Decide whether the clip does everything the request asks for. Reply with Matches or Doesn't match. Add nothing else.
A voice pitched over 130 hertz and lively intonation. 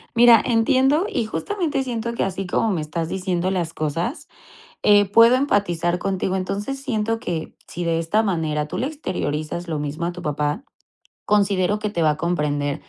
Matches